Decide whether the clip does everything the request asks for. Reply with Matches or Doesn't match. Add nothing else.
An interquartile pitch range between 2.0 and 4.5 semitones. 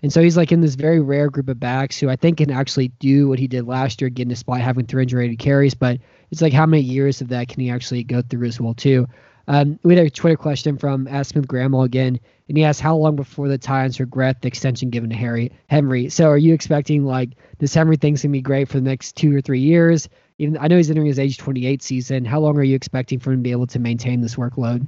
Matches